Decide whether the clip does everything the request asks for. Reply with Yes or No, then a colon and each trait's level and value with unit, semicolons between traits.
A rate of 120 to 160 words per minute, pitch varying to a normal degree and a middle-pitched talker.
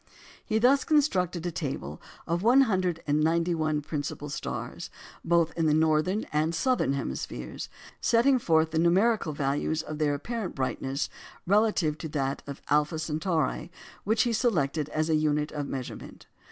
Yes: average, 150 wpm; average, 4.1 semitones; medium, 160 Hz